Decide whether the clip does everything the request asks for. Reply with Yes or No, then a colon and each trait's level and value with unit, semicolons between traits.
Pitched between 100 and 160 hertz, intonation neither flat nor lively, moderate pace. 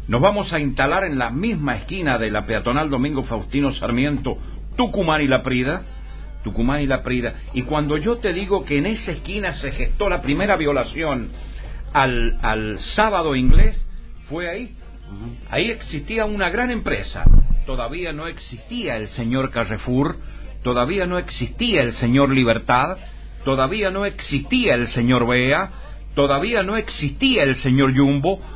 No: low, 135 Hz; wide, 6.3 semitones; average, 150 wpm